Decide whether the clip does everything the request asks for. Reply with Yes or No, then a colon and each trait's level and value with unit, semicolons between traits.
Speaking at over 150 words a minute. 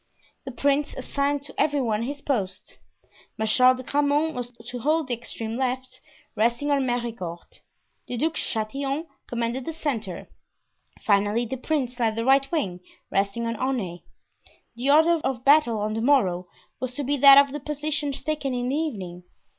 Yes: average, 170 wpm